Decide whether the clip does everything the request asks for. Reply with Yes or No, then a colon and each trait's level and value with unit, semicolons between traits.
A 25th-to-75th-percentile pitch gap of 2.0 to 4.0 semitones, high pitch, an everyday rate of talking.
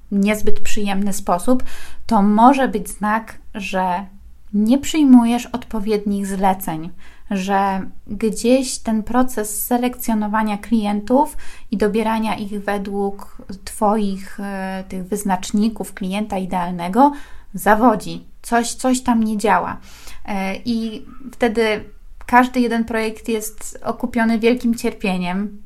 No: average, 2.8 semitones; high, 215 Hz; slow, 100 wpm